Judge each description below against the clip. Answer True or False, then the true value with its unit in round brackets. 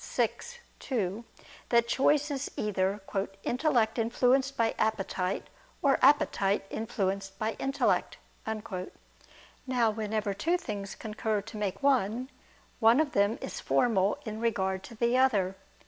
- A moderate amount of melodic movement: True (4.2 semitones)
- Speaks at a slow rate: True (125 wpm)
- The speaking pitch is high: True (220 Hz)